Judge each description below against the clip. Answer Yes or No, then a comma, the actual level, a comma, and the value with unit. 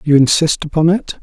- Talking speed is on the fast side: No, average, 195 wpm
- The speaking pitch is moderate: Yes, medium, 155 Hz